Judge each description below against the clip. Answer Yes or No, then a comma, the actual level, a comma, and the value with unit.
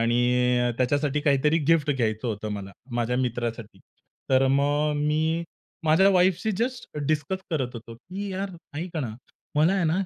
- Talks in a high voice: No, medium, 145 Hz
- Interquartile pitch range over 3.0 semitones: Yes, average, 5.0 semitones